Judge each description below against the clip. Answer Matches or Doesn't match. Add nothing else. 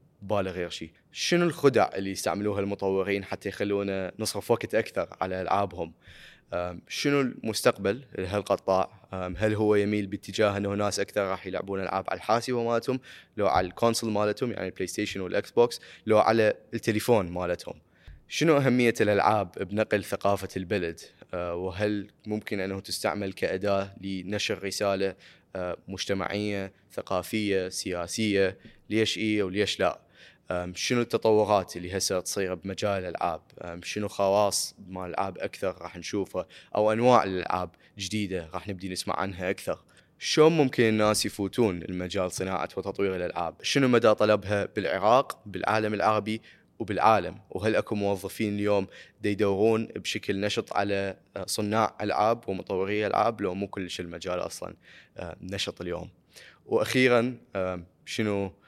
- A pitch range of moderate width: Doesn't match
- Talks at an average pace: Matches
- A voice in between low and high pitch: Doesn't match